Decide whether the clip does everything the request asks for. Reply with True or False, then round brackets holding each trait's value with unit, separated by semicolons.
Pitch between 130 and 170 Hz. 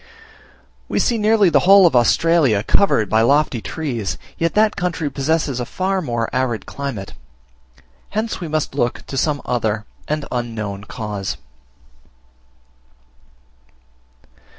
True (140 Hz)